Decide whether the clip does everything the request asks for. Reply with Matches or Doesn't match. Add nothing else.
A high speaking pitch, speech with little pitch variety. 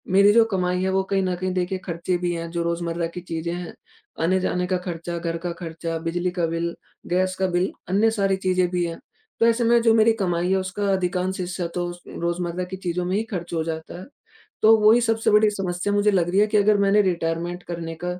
Doesn't match